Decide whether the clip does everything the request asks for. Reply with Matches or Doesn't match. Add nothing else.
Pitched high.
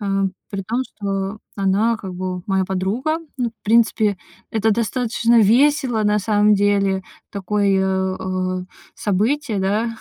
Matches